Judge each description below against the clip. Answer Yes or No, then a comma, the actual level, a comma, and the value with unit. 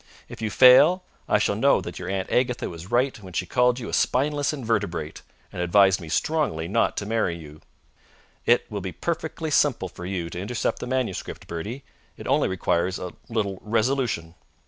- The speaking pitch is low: Yes, low, 105 Hz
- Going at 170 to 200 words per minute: Yes, average, 185 wpm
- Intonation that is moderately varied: No, wide, 6.0 semitones